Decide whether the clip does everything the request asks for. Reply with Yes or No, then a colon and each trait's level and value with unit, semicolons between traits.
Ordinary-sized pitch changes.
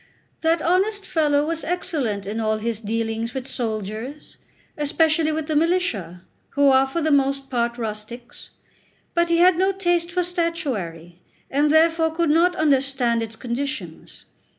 No: wide, 6.4 semitones